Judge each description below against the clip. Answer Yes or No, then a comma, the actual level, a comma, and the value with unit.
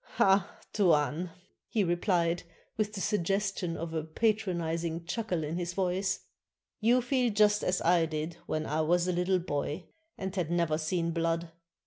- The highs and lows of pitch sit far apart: No, average, 2.9 semitones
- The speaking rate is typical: Yes, average, 160 wpm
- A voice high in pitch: No, medium, 175 Hz